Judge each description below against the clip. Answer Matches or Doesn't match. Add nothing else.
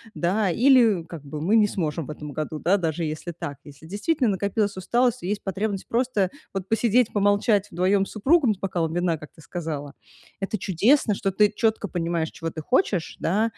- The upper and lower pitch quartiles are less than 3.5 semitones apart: Doesn't match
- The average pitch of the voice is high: Matches